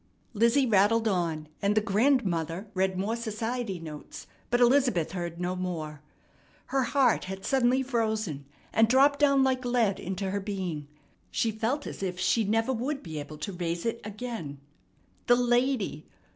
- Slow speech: No, average, 160 wpm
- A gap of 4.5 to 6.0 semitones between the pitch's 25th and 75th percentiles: Yes, average, 5.2 semitones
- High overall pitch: Yes, high, 215 Hz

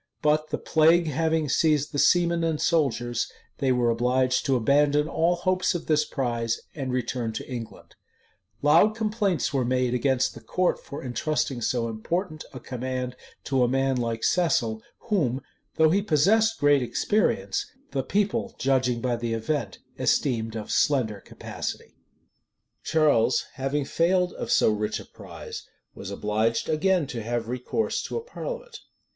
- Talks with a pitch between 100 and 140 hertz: Yes, low, 135 Hz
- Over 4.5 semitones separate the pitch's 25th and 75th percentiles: Yes, average, 5.2 semitones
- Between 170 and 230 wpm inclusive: No, average, 155 wpm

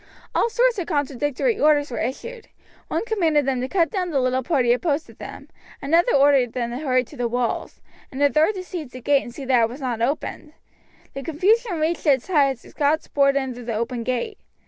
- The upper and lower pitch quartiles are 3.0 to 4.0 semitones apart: No, average, 4.6 semitones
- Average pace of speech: No, fast, 220 wpm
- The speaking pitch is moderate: No, very high, 280 Hz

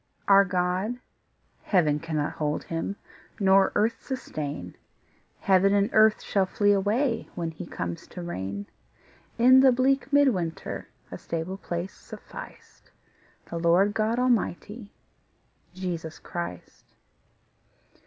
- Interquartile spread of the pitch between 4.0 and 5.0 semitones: Yes, average, 4.6 semitones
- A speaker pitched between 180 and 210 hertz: Yes, high, 190 Hz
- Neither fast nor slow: No, slow, 115 wpm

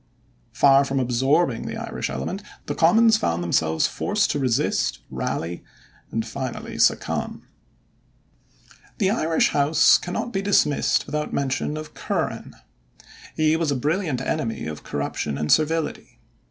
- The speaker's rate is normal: No, slow, 130 wpm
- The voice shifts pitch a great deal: Yes, wide, 6.2 semitones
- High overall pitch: No, medium, 140 Hz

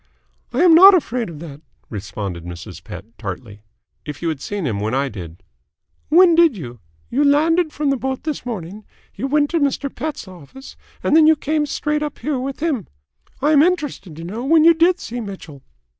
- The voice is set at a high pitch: Yes, very high, 260 Hz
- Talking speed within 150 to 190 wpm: No, average, 200 wpm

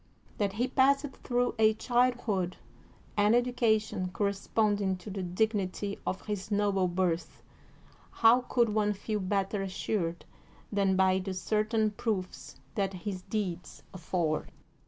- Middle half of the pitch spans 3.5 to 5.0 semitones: No, average, 2.7 semitones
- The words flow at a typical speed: No, slow, 130 wpm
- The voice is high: Yes, high, 205 Hz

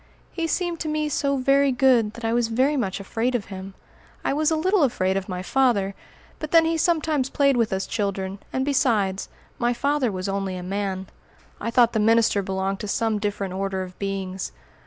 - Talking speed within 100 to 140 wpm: No, average, 200 wpm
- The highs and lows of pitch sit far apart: Yes, wide, 6.0 semitones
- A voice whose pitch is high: Yes, high, 225 Hz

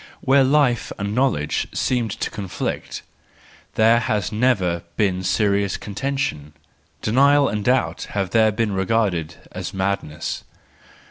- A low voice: Yes, low, 105 Hz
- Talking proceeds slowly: Yes, slow, 125 wpm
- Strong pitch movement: No, average, 4.6 semitones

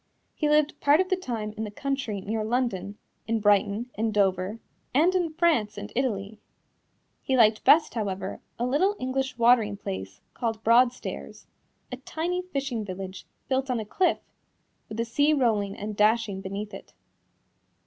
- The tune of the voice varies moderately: Yes, average, 4.7 semitones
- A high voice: Yes, high, 225 Hz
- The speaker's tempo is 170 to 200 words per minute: No, average, 160 wpm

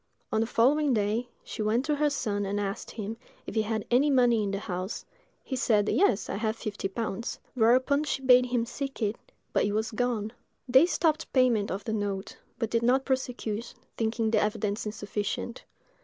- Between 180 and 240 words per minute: Yes, average, 190 wpm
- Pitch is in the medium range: No, high, 225 Hz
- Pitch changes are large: No, average, 3.3 semitones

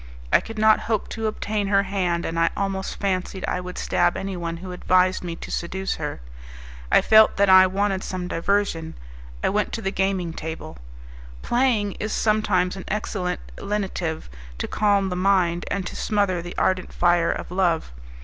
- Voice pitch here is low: No, high, 190 Hz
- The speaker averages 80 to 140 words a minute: No, average, 175 wpm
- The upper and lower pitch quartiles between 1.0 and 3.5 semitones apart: Yes, narrow, 2.5 semitones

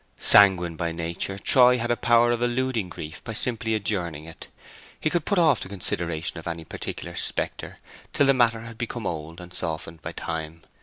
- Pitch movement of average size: No, wide, 6.3 semitones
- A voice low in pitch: Yes, very low, 95 Hz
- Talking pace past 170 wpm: Yes, average, 190 wpm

